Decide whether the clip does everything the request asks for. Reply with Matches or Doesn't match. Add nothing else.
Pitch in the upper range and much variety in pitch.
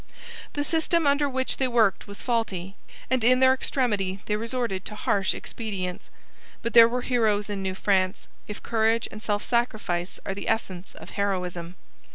Doesn't match